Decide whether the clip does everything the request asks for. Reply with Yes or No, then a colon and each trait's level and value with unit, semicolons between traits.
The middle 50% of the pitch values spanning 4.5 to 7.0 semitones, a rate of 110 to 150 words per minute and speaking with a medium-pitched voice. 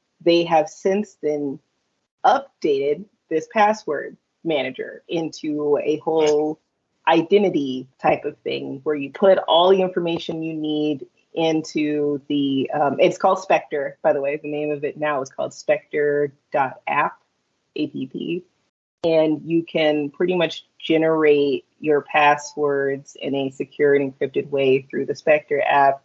No: average, 2.9 semitones; slow, 135 wpm; medium, 155 Hz